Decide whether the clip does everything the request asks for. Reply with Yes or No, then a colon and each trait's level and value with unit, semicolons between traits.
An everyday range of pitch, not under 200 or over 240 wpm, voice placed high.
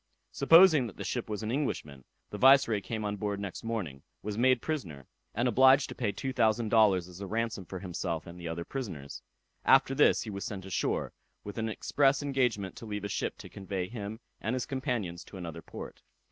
No: average, 4.9 semitones; fast, 205 wpm; low, 105 Hz